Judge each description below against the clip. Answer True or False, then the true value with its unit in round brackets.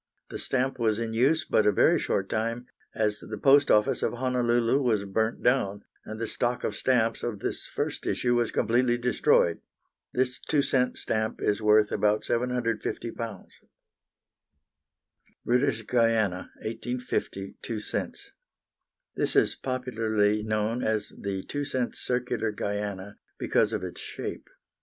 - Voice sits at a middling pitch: False (115 Hz)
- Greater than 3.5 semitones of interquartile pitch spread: False (2.8 semitones)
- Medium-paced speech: True (145 wpm)